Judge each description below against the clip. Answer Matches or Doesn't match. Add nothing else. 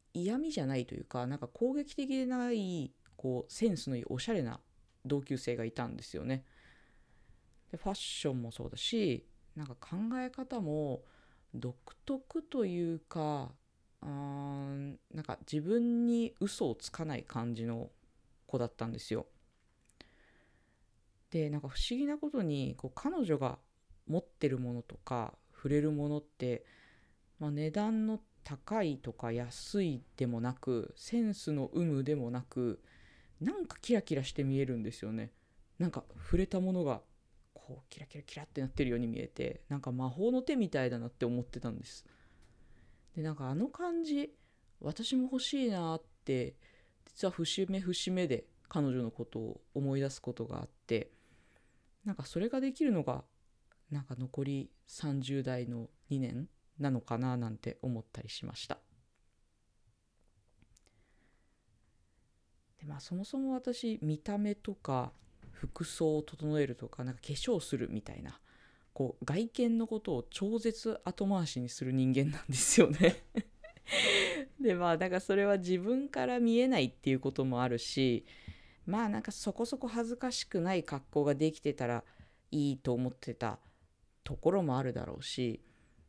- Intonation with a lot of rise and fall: Matches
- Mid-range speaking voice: Matches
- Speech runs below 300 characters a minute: Matches